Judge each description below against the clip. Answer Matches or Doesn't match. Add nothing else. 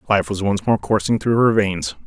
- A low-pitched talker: Matches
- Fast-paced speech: Matches